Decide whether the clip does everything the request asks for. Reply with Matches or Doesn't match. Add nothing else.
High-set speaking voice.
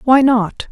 Matches